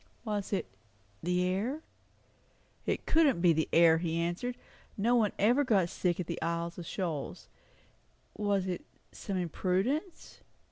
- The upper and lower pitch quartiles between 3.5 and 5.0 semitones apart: Yes, average, 4.2 semitones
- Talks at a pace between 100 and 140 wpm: Yes, slow, 135 wpm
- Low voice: No, medium, 185 Hz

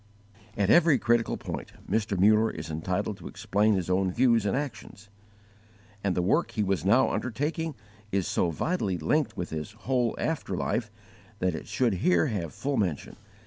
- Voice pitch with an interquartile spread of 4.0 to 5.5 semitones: Yes, average, 5.0 semitones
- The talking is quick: No, average, 170 wpm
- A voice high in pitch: No, low, 105 Hz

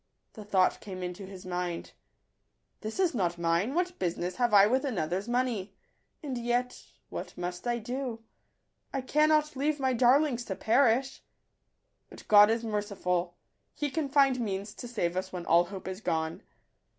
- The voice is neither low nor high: No, high, 220 Hz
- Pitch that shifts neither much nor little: No, wide, 5.8 semitones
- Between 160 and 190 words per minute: Yes, average, 175 wpm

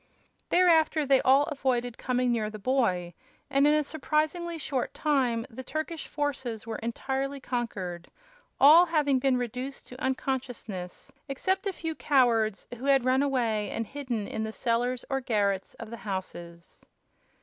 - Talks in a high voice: Yes, very high, 255 Hz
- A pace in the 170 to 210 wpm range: No, average, 150 wpm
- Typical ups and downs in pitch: Yes, average, 3.9 semitones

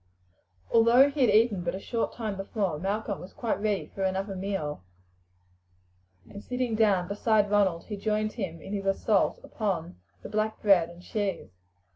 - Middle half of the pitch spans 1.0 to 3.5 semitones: Yes, narrow, 2.4 semitones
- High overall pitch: Yes, high, 200 Hz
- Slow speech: No, average, 165 wpm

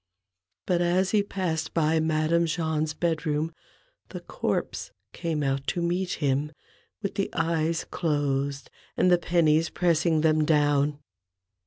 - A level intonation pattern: Yes, narrow, 2.3 semitones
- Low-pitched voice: No, medium, 160 Hz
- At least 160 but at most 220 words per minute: No, slow, 135 wpm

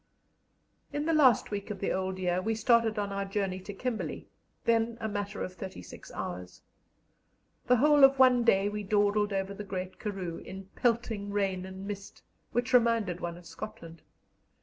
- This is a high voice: Yes, high, 205 Hz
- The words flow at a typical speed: Yes, average, 175 wpm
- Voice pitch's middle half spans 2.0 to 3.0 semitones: No, average, 3.4 semitones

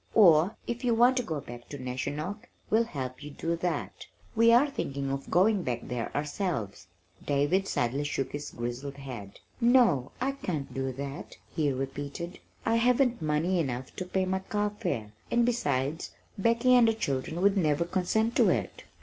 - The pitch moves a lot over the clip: Yes, wide, 8.3 semitones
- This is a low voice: No, medium, 165 Hz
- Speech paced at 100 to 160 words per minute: No, average, 170 wpm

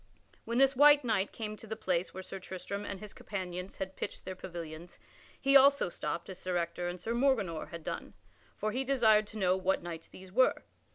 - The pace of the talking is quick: Yes, fast, 210 wpm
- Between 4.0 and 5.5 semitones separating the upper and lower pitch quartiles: Yes, average, 4.4 semitones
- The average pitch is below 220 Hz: Yes, high, 190 Hz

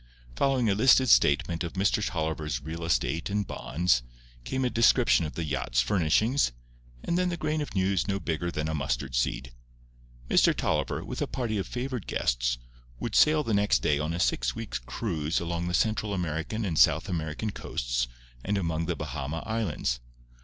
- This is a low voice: Yes, very low, 85 Hz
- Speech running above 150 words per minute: Yes, average, 180 wpm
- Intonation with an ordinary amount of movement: No, wide, 6.3 semitones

